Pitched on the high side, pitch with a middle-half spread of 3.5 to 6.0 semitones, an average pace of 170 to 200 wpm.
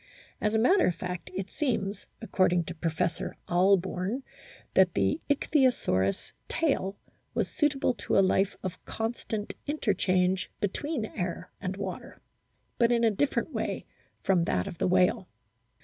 No: high, 195 Hz; average, 4.5 semitones; average, 140 wpm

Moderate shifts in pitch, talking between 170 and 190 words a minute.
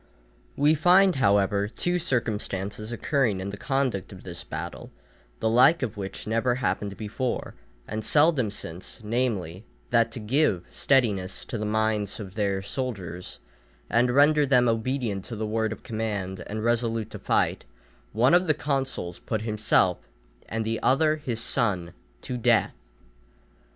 No: average, 4.2 semitones; average, 150 wpm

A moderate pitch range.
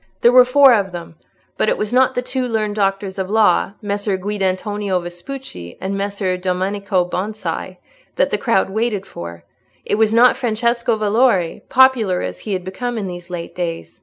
Yes: average, 3.9 semitones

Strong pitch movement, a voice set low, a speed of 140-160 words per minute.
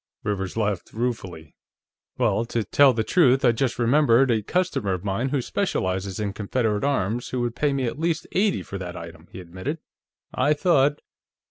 No: wide, 5.9 semitones; low, 115 Hz; average, 175 wpm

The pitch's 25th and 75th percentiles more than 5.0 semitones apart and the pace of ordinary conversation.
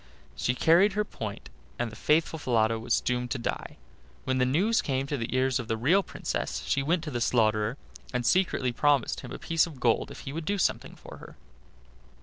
No: wide, 5.4 semitones; fast, 210 wpm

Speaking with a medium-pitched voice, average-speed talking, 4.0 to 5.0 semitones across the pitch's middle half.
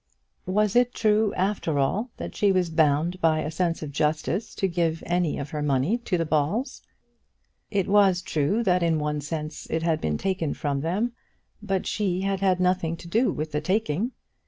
Yes: medium, 175 Hz; average, 190 wpm; average, 4.3 semitones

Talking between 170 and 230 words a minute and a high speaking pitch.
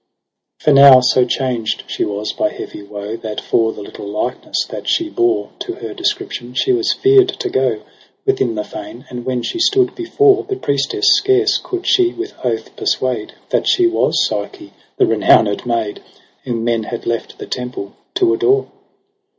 No: average, 175 wpm; low, 130 Hz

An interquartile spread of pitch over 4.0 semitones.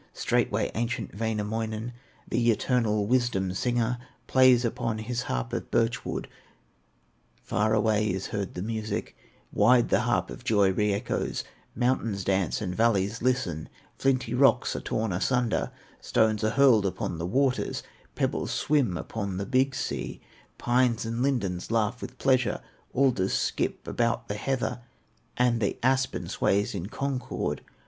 No: average, 3.3 semitones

